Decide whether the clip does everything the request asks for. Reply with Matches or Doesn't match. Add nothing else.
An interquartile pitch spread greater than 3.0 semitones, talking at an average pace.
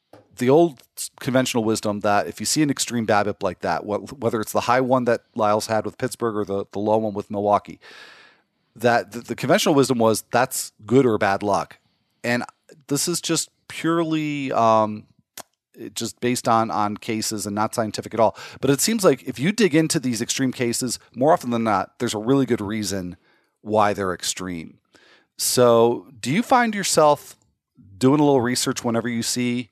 Matches